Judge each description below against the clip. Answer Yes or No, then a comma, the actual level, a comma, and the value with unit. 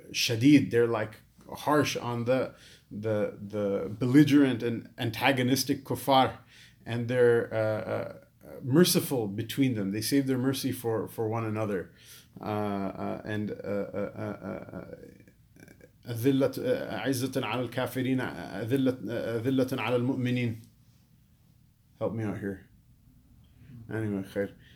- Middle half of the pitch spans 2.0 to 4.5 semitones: Yes, average, 3.5 semitones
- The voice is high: No, low, 120 Hz